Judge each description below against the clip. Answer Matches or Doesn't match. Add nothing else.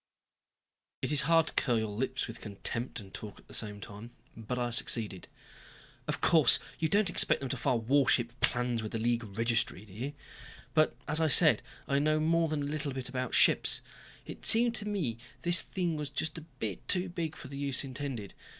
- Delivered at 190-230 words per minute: Matches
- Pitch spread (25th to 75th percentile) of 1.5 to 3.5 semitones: Doesn't match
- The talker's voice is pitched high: Doesn't match